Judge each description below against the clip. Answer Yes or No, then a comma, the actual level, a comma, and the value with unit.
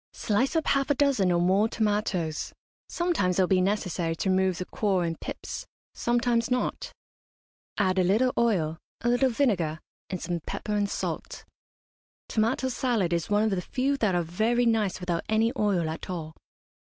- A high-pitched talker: Yes, high, 205 Hz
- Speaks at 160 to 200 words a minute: Yes, average, 175 wpm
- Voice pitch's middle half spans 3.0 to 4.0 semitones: No, average, 4.8 semitones